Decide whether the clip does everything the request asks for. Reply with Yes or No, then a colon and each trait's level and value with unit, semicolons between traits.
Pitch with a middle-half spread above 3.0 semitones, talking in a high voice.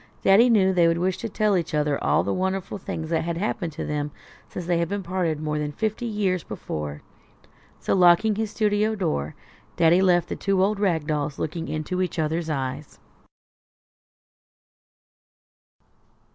No: average, 4.2 semitones; medium, 175 Hz